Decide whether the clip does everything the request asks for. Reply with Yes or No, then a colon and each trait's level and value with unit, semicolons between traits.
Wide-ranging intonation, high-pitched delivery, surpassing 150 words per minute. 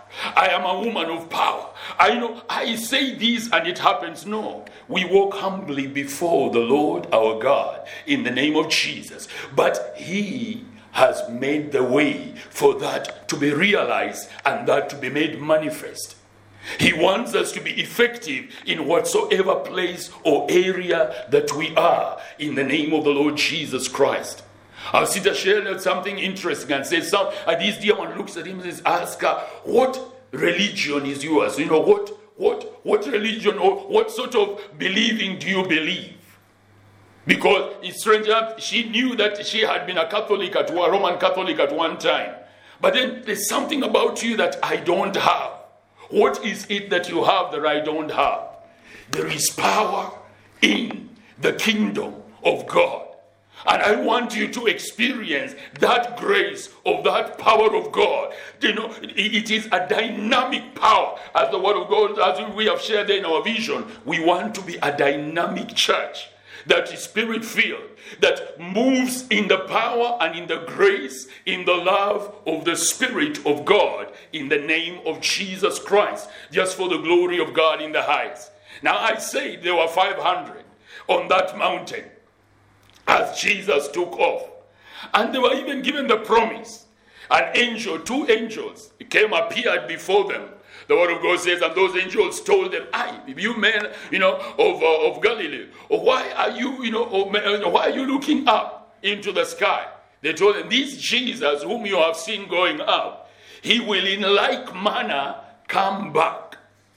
Yes: wide, 7.4 semitones; high, 215 Hz; average, 170 wpm